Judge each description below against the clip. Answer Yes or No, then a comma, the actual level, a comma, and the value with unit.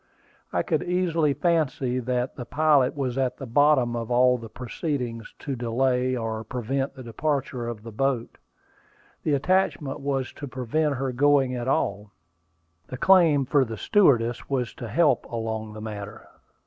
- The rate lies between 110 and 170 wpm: Yes, average, 160 wpm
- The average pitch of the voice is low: Yes, low, 130 Hz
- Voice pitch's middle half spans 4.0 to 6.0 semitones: No, average, 3.5 semitones